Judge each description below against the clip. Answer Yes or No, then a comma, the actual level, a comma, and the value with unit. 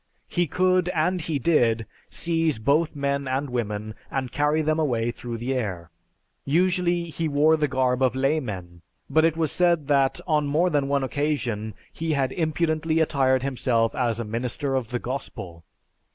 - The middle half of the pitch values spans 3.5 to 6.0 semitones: Yes, average, 4.5 semitones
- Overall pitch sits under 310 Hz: Yes, medium, 140 Hz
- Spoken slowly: No, average, 165 wpm